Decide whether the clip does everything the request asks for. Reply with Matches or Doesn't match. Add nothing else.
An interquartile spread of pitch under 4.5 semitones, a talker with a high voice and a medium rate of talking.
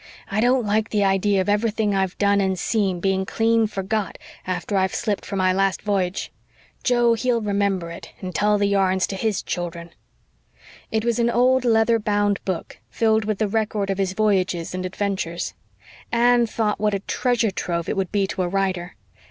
Matches